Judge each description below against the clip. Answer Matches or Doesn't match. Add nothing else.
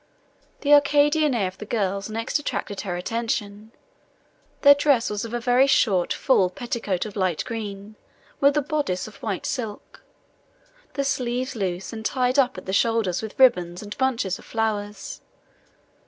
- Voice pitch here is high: Matches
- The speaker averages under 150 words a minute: Doesn't match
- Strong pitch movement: Doesn't match